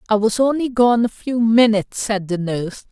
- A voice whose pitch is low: No, high, 220 Hz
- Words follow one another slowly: No, fast, 205 wpm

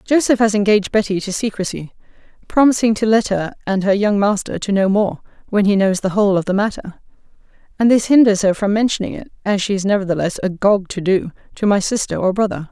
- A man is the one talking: No, female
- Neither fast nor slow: No, fast, 210 wpm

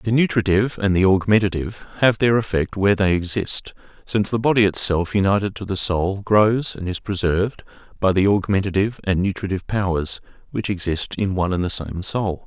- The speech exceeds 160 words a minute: Yes, average, 180 wpm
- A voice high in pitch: No, low, 100 Hz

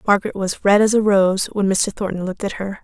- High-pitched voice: Yes, high, 200 Hz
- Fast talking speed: Yes, fast, 255 wpm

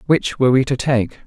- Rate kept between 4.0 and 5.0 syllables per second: No, 5.9 syllables/s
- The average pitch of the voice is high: No, low, 130 Hz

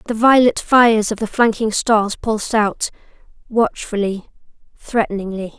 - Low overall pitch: No, high, 220 Hz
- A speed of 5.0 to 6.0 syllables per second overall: No, 4.6 syllables/s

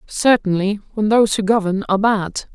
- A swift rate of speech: No, average, 165 wpm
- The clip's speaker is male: No, female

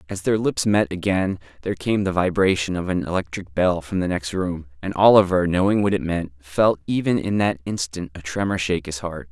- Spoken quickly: Yes, fast, 210 wpm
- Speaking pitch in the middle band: No, very low, 90 Hz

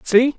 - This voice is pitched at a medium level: No, very high, 250 Hz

